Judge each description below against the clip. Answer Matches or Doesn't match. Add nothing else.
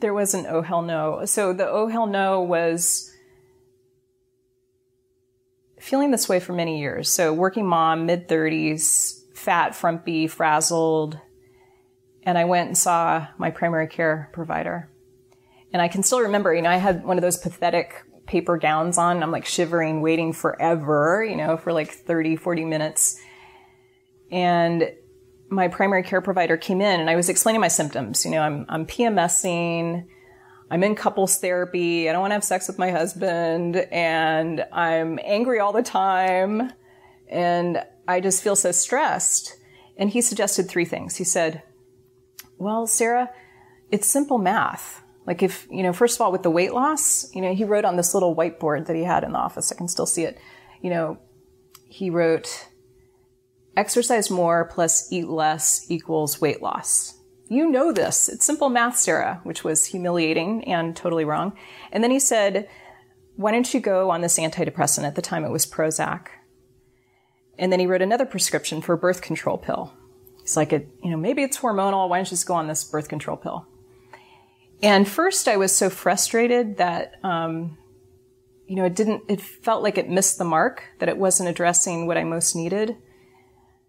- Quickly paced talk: Doesn't match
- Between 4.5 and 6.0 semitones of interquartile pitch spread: Doesn't match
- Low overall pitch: Doesn't match